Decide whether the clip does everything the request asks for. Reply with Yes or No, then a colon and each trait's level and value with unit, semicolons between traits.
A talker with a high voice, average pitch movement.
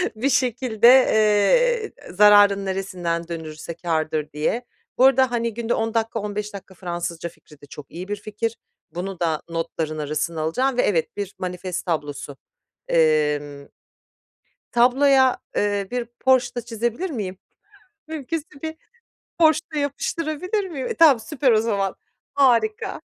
No: high, 210 Hz; wide, 7.2 semitones